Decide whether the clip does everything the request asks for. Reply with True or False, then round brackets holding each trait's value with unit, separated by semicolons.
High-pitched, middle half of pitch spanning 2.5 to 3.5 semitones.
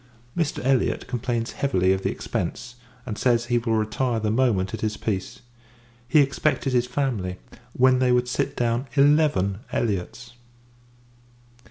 False (120 Hz; 3.2 semitones)